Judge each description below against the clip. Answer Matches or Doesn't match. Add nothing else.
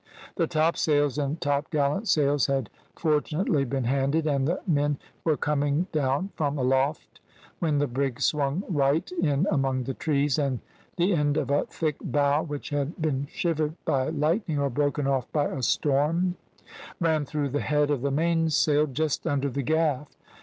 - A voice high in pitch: Doesn't match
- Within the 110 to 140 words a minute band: Doesn't match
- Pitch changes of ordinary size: Doesn't match